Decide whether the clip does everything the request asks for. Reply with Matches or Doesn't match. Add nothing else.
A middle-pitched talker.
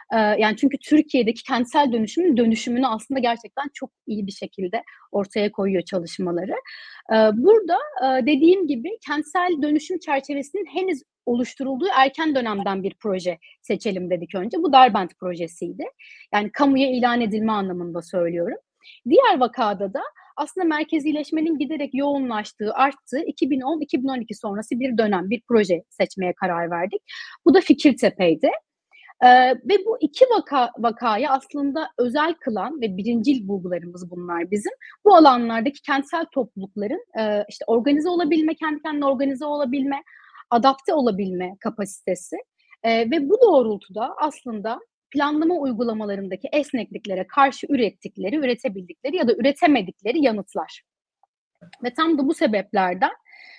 Doesn't match